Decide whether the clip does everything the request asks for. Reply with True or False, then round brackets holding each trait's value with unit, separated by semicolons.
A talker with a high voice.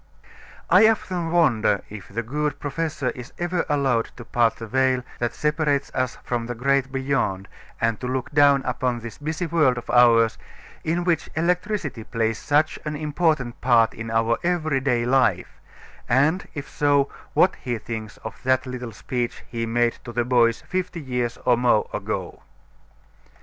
False (130 Hz)